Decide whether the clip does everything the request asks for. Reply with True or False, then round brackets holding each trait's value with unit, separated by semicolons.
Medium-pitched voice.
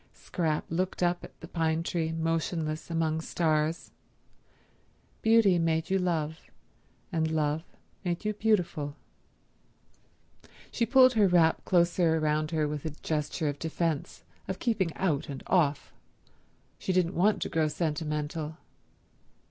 True (165 Hz)